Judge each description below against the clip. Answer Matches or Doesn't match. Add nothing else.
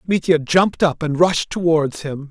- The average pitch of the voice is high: Doesn't match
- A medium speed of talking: Matches